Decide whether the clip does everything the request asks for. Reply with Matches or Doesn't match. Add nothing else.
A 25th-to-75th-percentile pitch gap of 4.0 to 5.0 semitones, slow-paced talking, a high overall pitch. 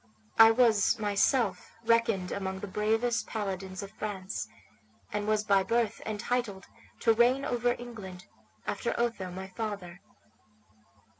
Doesn't match